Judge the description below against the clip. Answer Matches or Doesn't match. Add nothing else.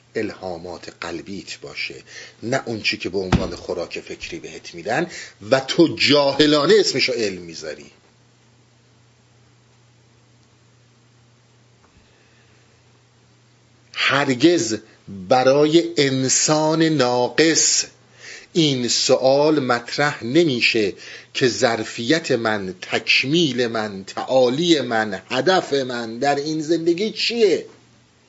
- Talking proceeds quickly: Doesn't match